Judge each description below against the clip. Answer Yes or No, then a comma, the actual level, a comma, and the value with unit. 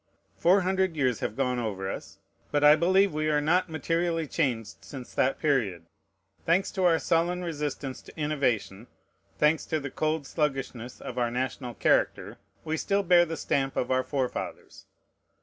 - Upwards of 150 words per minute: Yes, average, 165 wpm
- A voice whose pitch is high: No, medium, 150 Hz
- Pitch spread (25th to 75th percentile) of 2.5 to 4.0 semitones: No, average, 4.4 semitones